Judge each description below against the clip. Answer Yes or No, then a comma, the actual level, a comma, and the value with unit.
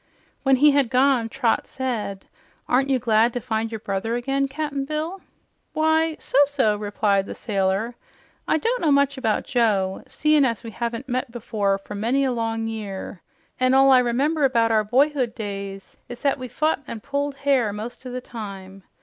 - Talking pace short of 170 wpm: No, average, 185 wpm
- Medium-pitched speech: No, high, 245 Hz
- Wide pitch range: No, average, 4.2 semitones